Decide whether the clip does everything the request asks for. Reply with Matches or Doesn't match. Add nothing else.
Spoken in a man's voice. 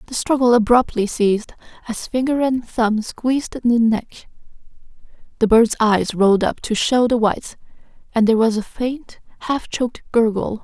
Doesn't match